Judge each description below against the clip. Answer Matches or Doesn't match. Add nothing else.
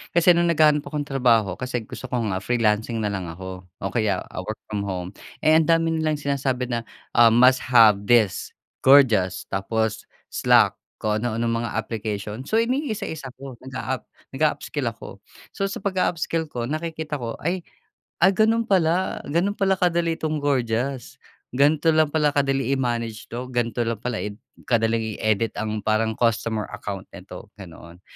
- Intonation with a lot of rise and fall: Matches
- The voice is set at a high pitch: Doesn't match